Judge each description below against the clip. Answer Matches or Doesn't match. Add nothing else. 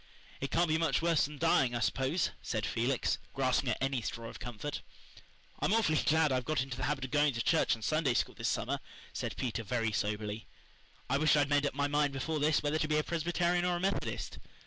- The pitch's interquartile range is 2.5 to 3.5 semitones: Doesn't match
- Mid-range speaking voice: Matches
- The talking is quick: Matches